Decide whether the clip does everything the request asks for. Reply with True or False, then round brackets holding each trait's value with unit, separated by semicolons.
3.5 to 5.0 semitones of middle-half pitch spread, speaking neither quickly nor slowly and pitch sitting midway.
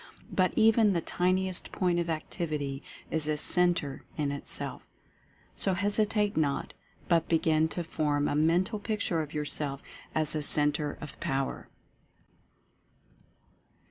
False (3.8 semitones; 130 wpm; 160 Hz)